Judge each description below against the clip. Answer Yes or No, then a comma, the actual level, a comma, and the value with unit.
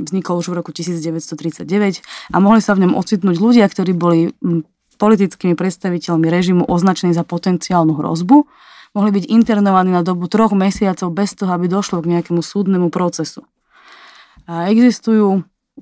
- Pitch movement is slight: No, average, 3.0 semitones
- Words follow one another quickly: No, average, 145 wpm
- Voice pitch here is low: No, medium, 185 Hz